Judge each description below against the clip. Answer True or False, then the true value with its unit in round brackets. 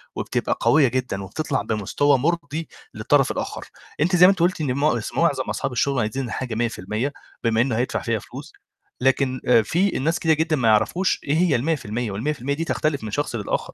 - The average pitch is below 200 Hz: True (135 Hz)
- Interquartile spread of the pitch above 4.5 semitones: True (5.1 semitones)